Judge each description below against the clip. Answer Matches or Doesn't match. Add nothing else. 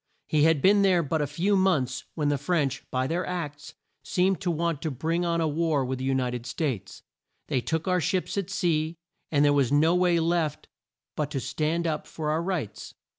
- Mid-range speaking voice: Matches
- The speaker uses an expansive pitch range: Doesn't match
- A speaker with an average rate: Doesn't match